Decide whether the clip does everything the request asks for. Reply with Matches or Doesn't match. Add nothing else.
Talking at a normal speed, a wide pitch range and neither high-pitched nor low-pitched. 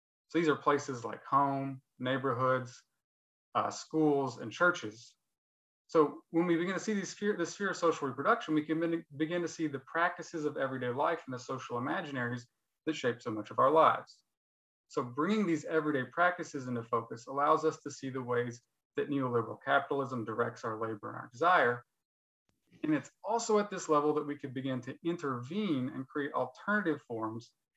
Doesn't match